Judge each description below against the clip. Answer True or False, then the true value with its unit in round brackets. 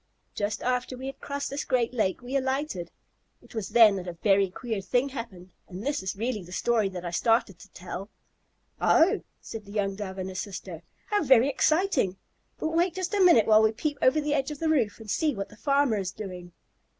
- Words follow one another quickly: True (220 wpm)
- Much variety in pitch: True (6.3 semitones)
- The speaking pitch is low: False (225 Hz)